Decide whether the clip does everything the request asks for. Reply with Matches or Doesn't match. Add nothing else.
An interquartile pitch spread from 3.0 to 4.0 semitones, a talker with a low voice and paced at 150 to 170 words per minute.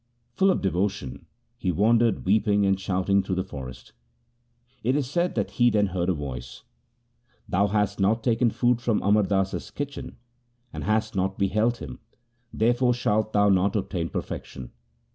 Matches